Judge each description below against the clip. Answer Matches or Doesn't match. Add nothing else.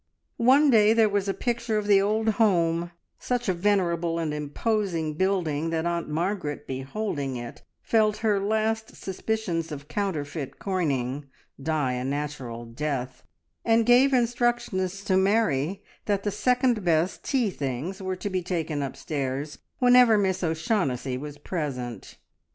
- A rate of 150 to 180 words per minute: Doesn't match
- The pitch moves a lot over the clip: Matches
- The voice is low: Doesn't match